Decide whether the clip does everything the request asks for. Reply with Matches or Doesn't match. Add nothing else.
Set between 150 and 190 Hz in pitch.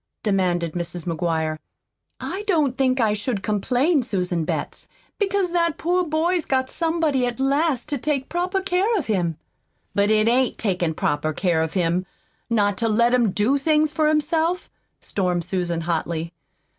Doesn't match